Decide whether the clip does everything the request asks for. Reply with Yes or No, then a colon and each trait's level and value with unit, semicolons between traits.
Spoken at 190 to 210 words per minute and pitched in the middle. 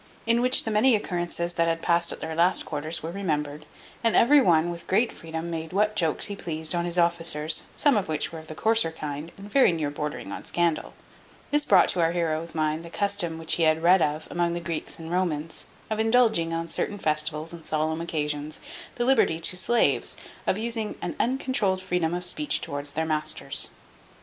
Yes: fast, 205 wpm; medium, 170 Hz